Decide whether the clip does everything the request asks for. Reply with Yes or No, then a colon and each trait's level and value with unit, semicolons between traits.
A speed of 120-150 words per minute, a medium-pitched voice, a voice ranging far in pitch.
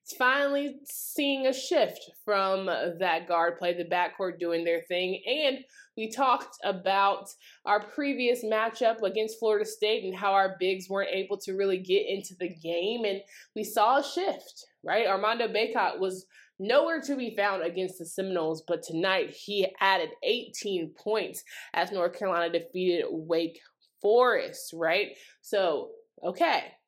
No: average, 145 wpm; high, 200 Hz; wide, 6.1 semitones